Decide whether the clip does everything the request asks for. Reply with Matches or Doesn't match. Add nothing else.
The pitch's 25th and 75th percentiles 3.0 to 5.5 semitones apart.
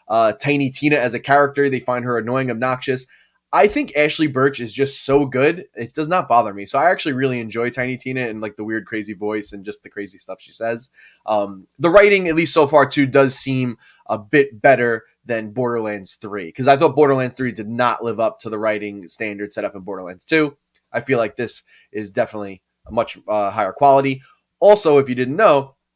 Matches